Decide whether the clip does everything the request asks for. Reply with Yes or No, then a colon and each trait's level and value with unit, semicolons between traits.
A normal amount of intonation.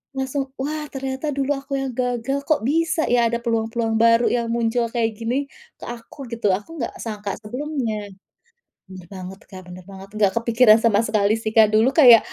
Yes: average, 3.8 semitones